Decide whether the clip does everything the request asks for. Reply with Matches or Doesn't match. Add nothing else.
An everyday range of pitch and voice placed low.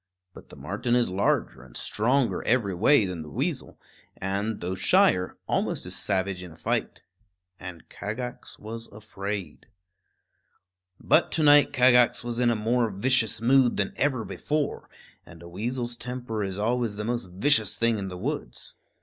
Matches